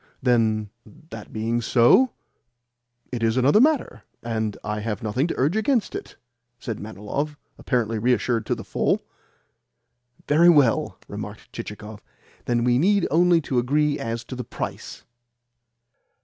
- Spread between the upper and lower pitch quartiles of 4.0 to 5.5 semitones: Yes, average, 5.1 semitones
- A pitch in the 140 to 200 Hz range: No, low, 120 Hz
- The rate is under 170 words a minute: Yes, slow, 135 wpm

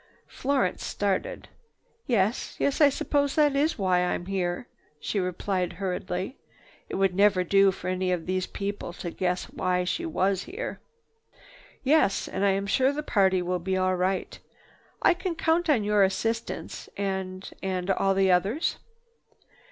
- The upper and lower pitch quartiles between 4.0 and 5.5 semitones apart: Yes, average, 4.5 semitones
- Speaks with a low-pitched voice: No, high, 195 Hz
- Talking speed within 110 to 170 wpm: Yes, average, 150 wpm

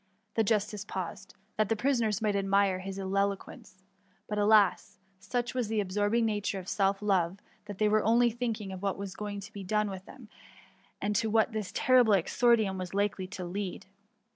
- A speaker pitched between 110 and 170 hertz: No, high, 205 Hz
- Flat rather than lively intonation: Yes, narrow, 2.0 semitones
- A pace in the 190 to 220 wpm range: Yes, average, 195 wpm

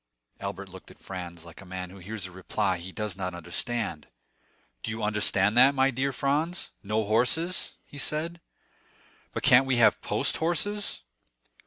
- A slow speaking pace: No, average, 160 wpm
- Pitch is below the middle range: Yes, low, 110 Hz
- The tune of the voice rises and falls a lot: Yes, wide, 6.5 semitones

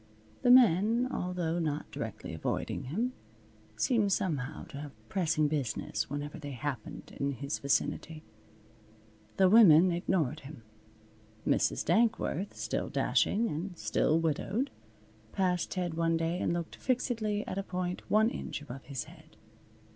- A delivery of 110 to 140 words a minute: Yes, slow, 135 wpm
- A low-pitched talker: No, medium, 165 Hz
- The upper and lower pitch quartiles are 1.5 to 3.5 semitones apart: No, average, 5.2 semitones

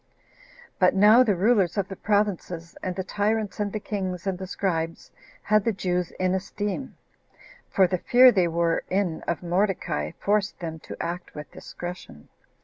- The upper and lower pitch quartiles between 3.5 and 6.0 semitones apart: No, average, 2.8 semitones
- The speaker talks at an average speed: Yes, average, 165 wpm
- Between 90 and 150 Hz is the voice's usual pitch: No, high, 190 Hz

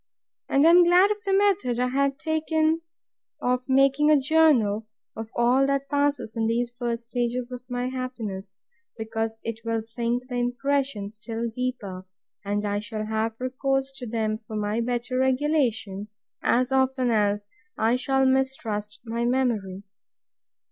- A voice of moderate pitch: No, high, 245 Hz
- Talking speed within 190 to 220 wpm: No, average, 150 wpm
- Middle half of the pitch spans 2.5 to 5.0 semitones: Yes, average, 3.4 semitones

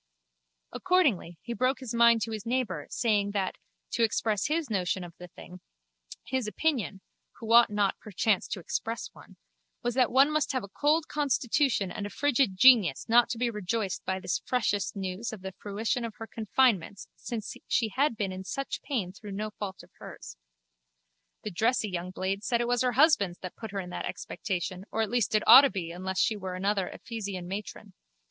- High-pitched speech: Yes, high, 215 Hz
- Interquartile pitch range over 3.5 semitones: Yes, average, 4.2 semitones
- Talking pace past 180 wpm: Yes, average, 195 wpm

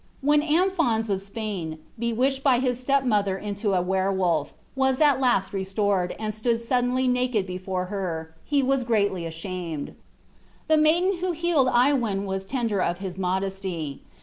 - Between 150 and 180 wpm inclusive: Yes, average, 155 wpm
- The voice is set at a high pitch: Yes, high, 215 Hz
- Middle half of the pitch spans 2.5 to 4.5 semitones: No, wide, 5.4 semitones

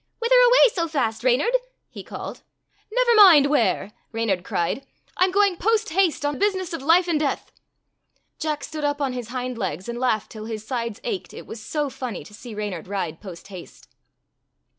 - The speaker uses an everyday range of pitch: No, wide, 8.7 semitones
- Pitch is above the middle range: Yes, very high, 270 Hz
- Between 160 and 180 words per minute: No, average, 190 wpm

